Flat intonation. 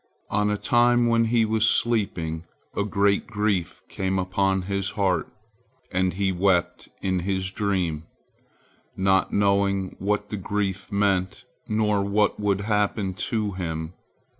Yes: narrow, 1.8 semitones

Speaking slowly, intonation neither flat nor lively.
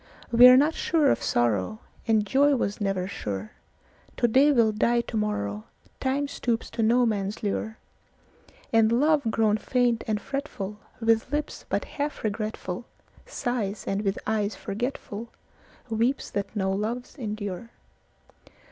Yes: slow, 120 wpm; average, 3.5 semitones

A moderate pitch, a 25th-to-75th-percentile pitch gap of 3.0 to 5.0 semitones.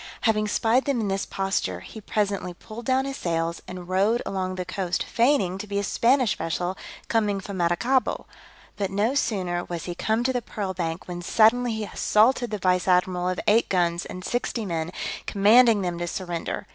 No: high, 195 Hz; average, 4.0 semitones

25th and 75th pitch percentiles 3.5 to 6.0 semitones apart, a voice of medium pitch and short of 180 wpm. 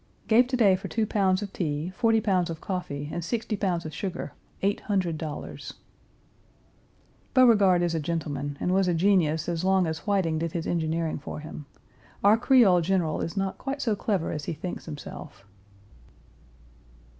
Yes: average, 4.0 semitones; medium, 180 Hz; average, 165 wpm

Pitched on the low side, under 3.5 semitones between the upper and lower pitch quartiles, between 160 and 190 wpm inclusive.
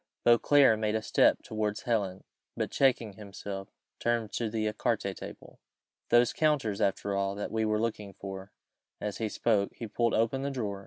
Yes: low, 110 Hz; average, 2.7 semitones; average, 180 wpm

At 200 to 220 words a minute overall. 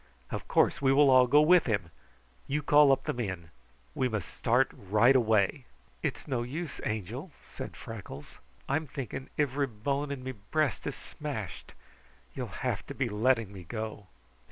No: average, 165 wpm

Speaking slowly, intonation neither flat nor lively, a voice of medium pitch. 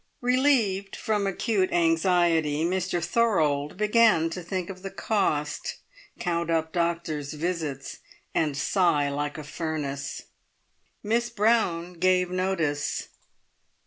Yes: slow, 110 wpm; average, 3.8 semitones; medium, 175 Hz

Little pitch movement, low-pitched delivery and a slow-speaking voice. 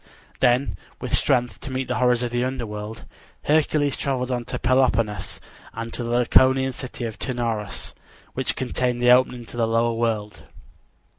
No: narrow, 2.0 semitones; low, 120 Hz; average, 160 wpm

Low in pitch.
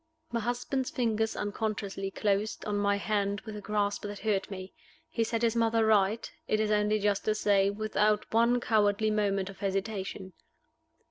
No: high, 210 Hz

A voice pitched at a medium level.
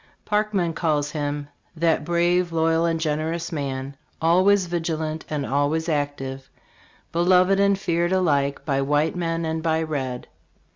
Yes: medium, 160 Hz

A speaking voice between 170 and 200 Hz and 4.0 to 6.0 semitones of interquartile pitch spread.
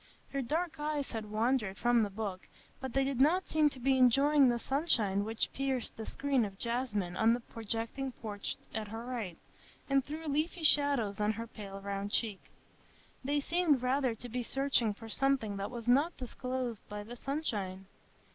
No: high, 245 Hz; average, 4.3 semitones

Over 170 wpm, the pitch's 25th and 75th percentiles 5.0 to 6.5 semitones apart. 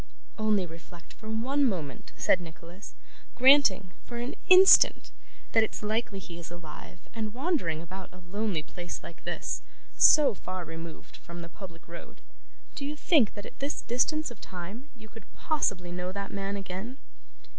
No: average, 165 wpm; wide, 5.6 semitones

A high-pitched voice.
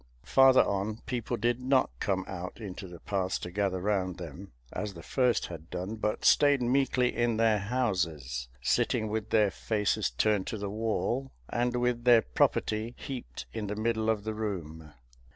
No: low, 105 Hz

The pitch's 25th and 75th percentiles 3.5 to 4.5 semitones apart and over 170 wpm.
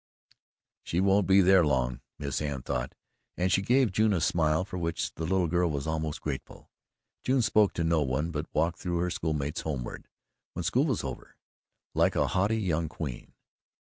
Yes: average, 3.9 semitones; average, 180 wpm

